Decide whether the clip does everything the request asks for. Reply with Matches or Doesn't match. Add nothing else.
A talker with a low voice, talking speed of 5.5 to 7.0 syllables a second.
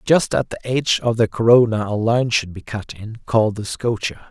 Doesn't match